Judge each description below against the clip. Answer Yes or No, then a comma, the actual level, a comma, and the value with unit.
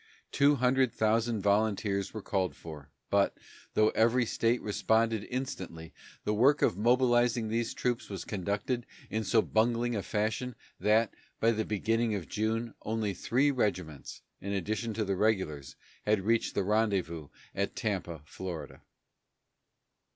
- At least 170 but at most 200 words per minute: No, average, 140 wpm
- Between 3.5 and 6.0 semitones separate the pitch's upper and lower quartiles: No, average, 2.9 semitones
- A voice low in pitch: Yes, low, 110 Hz